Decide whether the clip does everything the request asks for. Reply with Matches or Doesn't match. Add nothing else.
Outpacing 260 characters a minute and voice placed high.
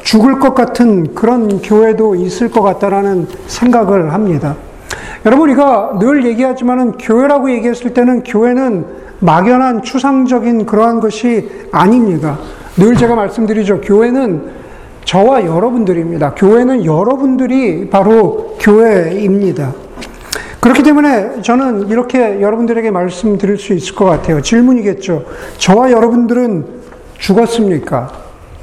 Matches